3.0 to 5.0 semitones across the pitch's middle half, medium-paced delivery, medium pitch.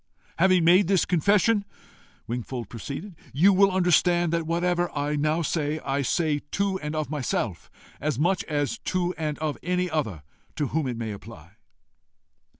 Yes: average, 4.0 semitones; average, 155 wpm; medium, 155 Hz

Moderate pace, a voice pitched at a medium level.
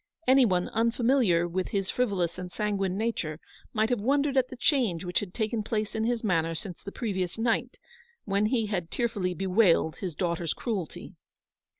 No: average, 175 wpm; high, 205 Hz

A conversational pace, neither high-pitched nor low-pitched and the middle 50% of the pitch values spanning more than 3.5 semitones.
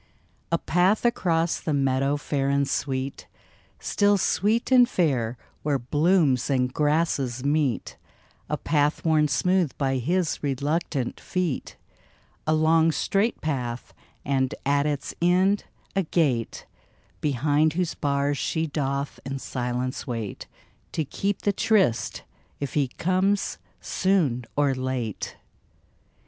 No: slow, 125 wpm; medium, 145 Hz; average, 4.3 semitones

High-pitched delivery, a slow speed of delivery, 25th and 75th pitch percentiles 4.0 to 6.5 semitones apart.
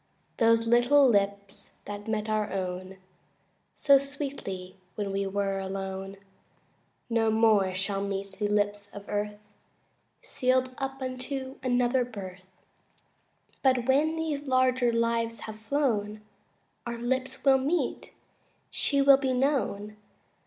Yes: high, 230 Hz; slow, 120 wpm; average, 4.6 semitones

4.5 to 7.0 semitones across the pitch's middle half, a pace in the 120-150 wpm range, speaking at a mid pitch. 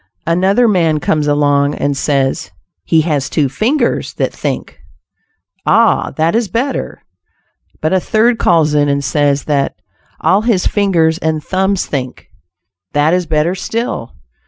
Yes: average, 4.8 semitones; average, 140 wpm; medium, 160 Hz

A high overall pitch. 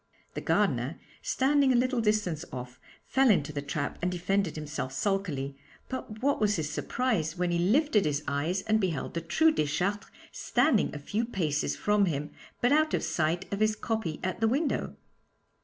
Yes: high, 195 Hz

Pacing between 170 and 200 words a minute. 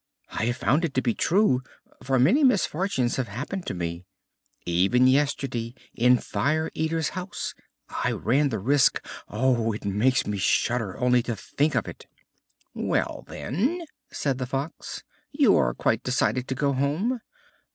No: average, 155 wpm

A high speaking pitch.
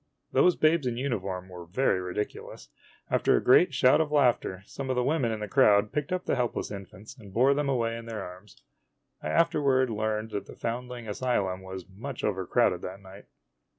No: low, 115 Hz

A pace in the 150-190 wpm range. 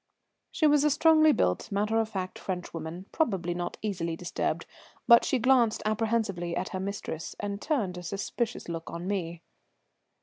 Yes: average, 165 wpm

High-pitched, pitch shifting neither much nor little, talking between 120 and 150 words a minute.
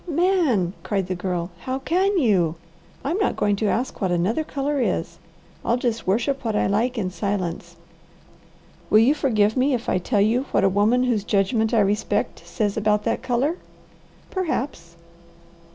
No: high, 220 Hz; average, 5.0 semitones; average, 170 wpm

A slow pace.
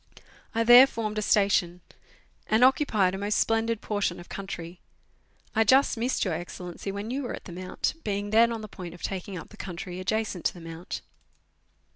No: average, 190 wpm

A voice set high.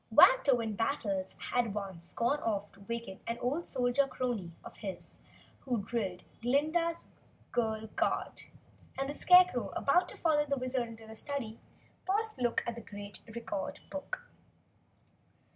Yes: high, 240 Hz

